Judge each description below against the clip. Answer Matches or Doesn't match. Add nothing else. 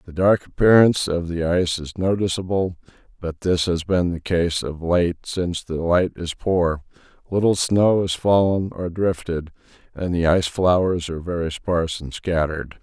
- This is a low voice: Matches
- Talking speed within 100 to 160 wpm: Doesn't match